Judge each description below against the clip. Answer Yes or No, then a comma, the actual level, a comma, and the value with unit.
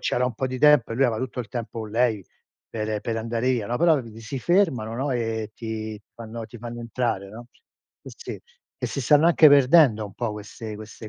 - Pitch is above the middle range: No, low, 115 Hz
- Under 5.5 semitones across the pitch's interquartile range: Yes, average, 2.7 semitones